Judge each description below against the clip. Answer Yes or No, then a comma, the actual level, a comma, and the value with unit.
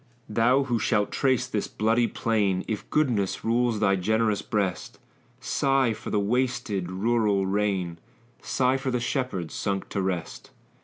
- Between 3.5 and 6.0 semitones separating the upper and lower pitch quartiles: Yes, average, 4.0 semitones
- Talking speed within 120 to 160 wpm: Yes, average, 145 wpm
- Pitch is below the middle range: Yes, low, 110 Hz